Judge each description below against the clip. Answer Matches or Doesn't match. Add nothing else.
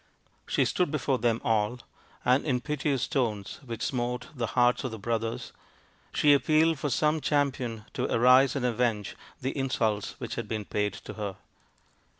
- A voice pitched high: Doesn't match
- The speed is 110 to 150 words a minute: Doesn't match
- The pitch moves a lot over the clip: Doesn't match